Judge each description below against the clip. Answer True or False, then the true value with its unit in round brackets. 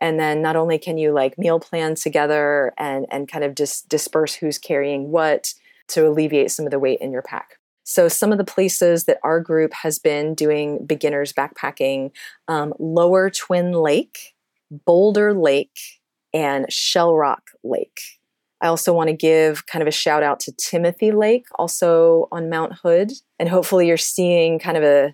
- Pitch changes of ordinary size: False (2.3 semitones)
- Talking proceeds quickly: False (180 wpm)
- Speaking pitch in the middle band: True (160 Hz)